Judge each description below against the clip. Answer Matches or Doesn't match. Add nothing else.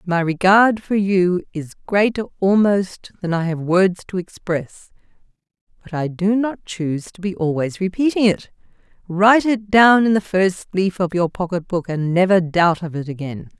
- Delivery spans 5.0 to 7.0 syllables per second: Doesn't match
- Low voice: Doesn't match